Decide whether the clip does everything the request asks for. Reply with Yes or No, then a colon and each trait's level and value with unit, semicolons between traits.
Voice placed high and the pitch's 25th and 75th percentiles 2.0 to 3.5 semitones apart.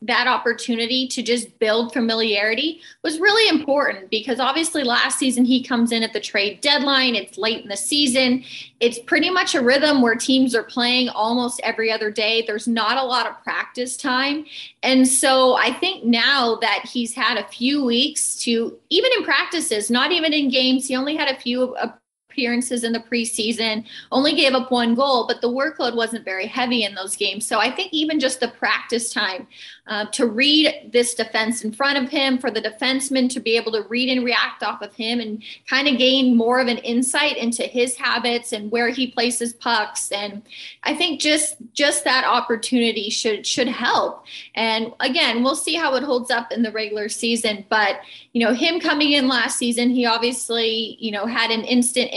Yes: high, 245 Hz; average, 2.7 semitones